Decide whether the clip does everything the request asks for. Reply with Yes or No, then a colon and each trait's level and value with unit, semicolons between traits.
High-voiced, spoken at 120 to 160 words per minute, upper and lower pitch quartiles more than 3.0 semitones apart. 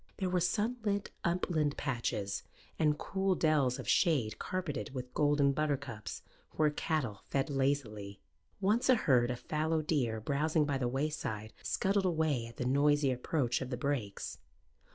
No: medium, 145 Hz; average, 150 wpm; average, 4.3 semitones